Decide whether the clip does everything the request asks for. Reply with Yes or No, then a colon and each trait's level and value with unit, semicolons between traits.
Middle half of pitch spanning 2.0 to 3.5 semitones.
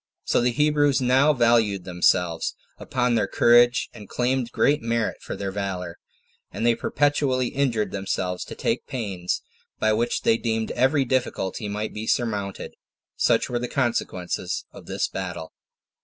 No: average, 4.3 semitones